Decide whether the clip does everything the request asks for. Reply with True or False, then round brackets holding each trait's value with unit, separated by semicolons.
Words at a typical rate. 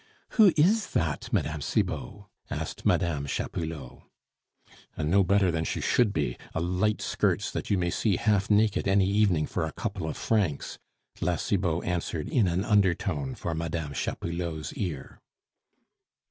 True (150 wpm)